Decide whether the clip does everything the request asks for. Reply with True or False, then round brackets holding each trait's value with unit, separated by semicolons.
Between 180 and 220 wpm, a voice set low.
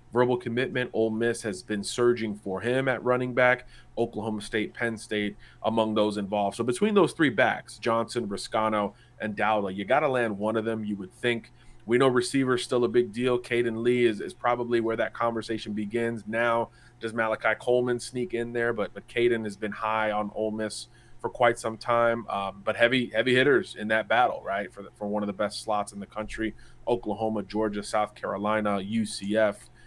True (200 wpm; 115 Hz)